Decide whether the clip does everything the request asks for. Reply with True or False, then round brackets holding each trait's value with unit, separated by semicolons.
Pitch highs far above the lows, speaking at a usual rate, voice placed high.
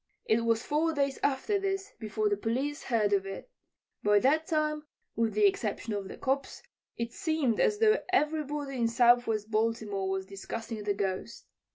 True (6.0 semitones; 170 wpm; 235 Hz)